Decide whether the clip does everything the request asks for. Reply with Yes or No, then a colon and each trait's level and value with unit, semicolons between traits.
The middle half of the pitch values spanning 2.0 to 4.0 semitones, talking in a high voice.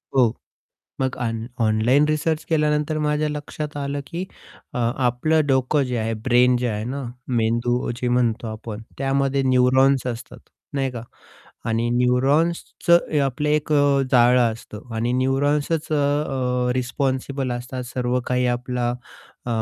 No: average, 2.8 semitones; low, 130 Hz